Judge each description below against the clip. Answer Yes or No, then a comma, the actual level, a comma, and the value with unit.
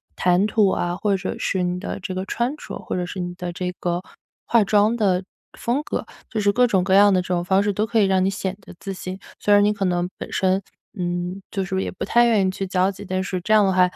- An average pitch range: No, narrow, 2.0 semitones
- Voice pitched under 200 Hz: Yes, high, 190 Hz